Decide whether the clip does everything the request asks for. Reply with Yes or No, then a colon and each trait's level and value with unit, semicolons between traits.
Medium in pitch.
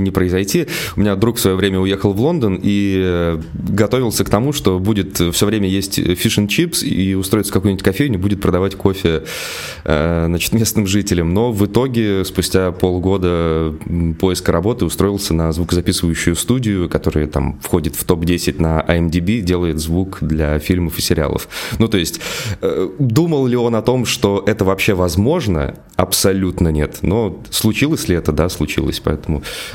No: very low, 95 Hz